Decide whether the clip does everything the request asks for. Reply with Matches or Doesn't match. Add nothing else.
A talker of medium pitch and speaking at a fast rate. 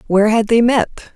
Doesn't match